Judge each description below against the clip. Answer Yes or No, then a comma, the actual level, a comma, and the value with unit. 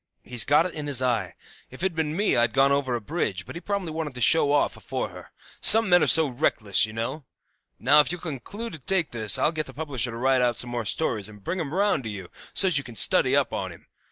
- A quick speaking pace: Yes, fast, 265 wpm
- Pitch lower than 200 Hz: Yes, medium, 140 Hz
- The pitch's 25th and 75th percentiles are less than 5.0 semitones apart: No, average, 5.3 semitones